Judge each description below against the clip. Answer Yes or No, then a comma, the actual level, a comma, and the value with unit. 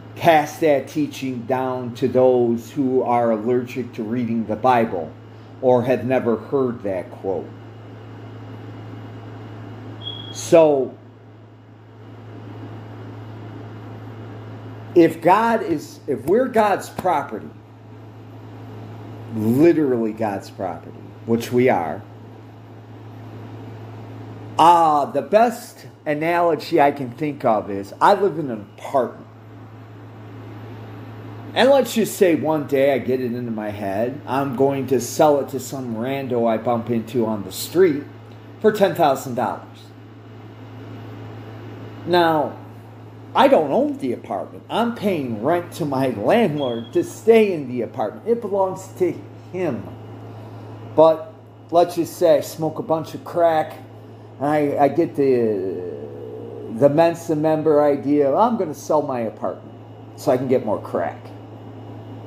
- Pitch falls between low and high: No, low, 115 Hz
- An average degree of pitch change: Yes, average, 4.5 semitones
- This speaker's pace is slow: Yes, slow, 125 wpm